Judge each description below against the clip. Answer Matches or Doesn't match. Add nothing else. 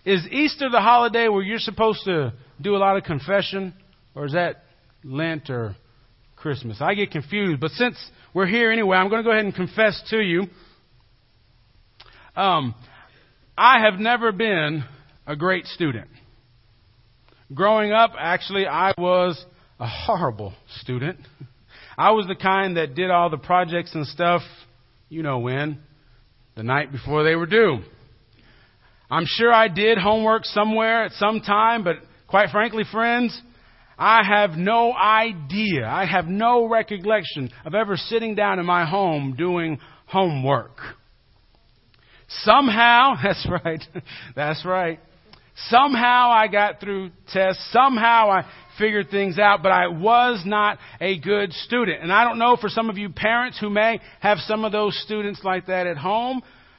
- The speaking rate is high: Doesn't match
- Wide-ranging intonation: Matches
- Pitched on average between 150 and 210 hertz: Matches